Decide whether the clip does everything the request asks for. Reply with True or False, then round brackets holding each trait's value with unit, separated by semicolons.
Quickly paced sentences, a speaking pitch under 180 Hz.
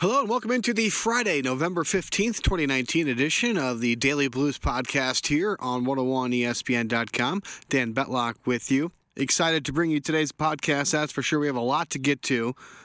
False (180 wpm; 140 Hz)